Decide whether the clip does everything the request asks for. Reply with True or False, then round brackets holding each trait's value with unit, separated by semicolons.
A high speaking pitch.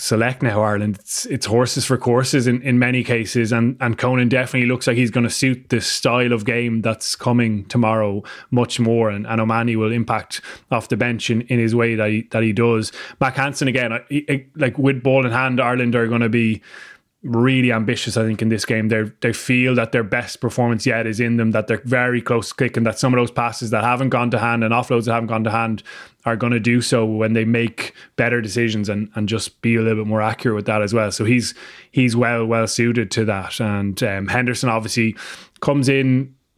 False (120 Hz)